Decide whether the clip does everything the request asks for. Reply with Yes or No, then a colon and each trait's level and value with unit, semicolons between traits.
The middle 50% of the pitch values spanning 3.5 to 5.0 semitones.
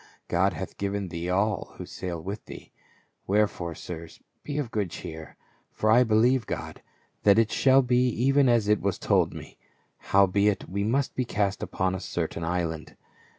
Yes: average, 4.6 semitones